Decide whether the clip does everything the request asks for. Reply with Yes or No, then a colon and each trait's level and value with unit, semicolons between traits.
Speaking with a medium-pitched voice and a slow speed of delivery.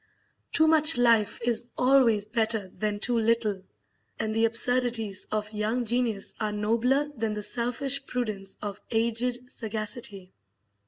No: high, 225 Hz; slow, 130 wpm